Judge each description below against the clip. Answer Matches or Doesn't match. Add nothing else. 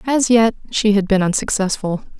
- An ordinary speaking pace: Matches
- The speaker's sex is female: Matches